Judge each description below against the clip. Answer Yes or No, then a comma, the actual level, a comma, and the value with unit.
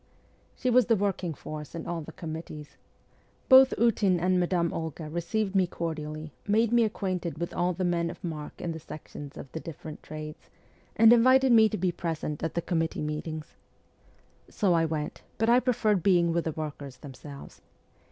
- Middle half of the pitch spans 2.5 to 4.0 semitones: No, average, 4.5 semitones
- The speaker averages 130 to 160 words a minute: No, average, 180 wpm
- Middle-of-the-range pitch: Yes, medium, 170 Hz